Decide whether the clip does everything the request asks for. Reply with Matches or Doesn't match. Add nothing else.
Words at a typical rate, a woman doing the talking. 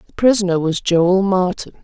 Matches